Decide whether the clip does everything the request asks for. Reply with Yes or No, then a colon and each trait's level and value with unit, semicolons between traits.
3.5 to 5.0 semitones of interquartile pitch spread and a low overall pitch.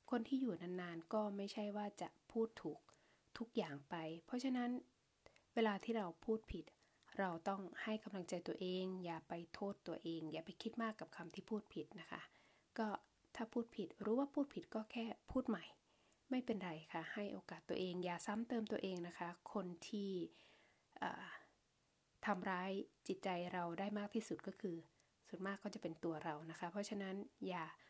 No: average, 4.2 semitones; high, 200 Hz